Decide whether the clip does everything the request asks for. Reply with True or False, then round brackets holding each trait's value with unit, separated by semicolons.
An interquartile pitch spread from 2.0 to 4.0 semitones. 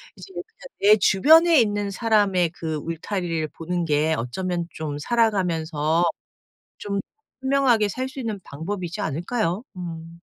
False (5.1 semitones)